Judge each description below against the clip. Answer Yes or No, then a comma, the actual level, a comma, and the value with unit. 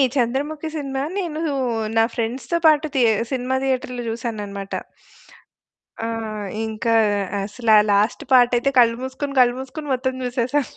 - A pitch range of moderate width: Yes, average, 3.0 semitones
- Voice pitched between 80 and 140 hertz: No, very high, 255 Hz